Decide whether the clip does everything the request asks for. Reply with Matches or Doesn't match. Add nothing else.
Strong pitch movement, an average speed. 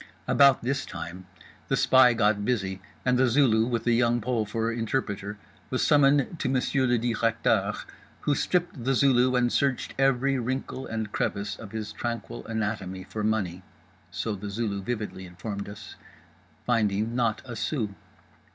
Doesn't match